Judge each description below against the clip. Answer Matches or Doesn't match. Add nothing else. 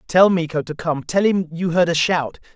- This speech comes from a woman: Doesn't match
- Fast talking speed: Matches